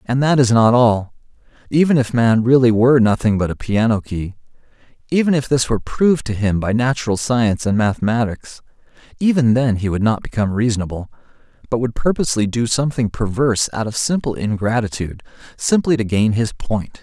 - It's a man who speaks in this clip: Yes, male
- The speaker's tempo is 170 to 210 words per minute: Yes, average, 175 wpm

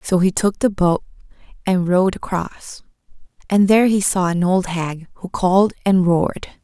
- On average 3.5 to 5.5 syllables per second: Yes, 4.9 syllables/s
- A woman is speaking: Yes, female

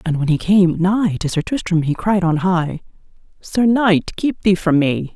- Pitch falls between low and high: Yes, medium, 180 Hz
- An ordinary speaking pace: No, fast, 210 wpm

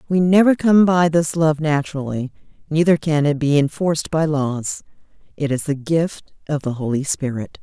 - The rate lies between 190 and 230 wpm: No, average, 175 wpm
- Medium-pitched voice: Yes, medium, 150 Hz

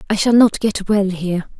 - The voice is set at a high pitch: Yes, high, 200 Hz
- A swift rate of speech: Yes, fast, 225 wpm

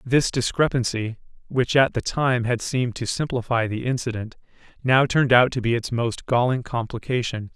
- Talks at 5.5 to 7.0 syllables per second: No, 5.1 syllables/s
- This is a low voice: Yes, low, 120 Hz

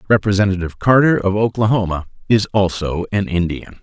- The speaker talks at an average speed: No, slow, 125 wpm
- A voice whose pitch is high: No, low, 100 Hz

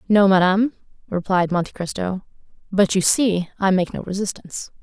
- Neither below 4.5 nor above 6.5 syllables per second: Yes, 5.4 syllables/s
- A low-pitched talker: No, high, 190 Hz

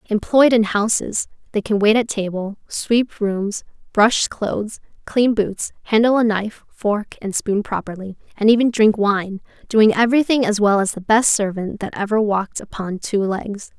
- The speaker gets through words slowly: No, average, 170 wpm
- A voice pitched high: Yes, high, 210 Hz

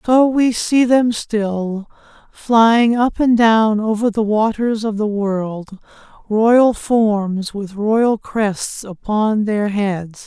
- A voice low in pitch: No, high, 215 Hz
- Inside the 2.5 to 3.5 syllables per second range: Yes, 2.8 syllables/s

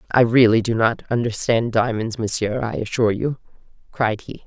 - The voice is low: Yes, low, 115 Hz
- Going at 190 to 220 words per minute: No, average, 160 wpm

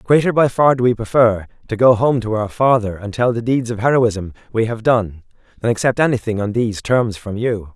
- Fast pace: Yes, fast, 225 wpm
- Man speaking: Yes, male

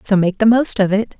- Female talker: Yes, female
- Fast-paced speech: Yes, fast, 300 wpm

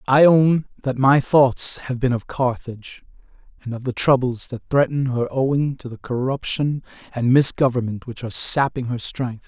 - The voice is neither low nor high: No, low, 130 Hz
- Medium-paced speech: Yes, average, 170 wpm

